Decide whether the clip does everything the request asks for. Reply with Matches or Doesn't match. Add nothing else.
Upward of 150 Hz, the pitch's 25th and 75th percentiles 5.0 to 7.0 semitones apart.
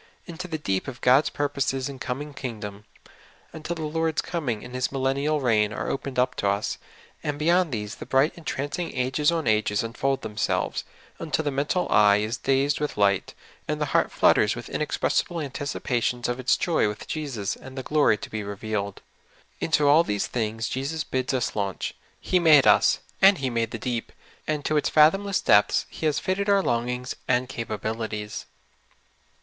Doesn't match